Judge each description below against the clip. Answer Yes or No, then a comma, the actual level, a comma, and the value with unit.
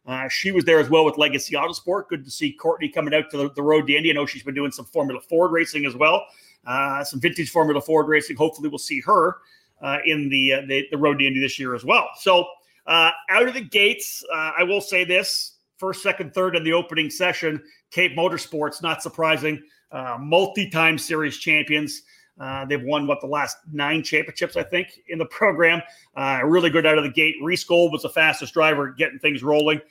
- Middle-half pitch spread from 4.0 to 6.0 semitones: No, average, 3.1 semitones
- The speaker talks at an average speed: No, fast, 220 wpm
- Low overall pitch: No, medium, 160 Hz